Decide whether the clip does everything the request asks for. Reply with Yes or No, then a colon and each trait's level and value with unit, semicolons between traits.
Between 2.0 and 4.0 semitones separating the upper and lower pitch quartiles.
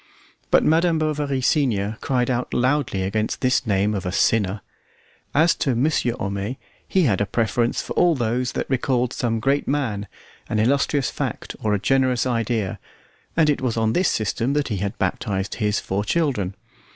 No: average, 4.8 semitones